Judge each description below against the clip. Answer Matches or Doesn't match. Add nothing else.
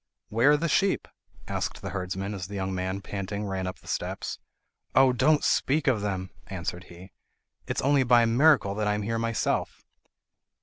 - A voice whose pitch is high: Doesn't match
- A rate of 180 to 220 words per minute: Matches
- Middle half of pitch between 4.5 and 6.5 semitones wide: Matches